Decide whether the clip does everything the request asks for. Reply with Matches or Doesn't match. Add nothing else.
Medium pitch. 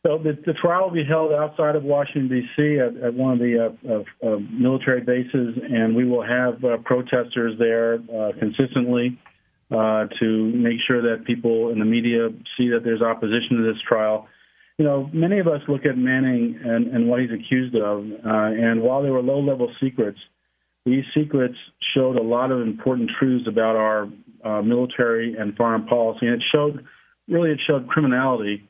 Doesn't match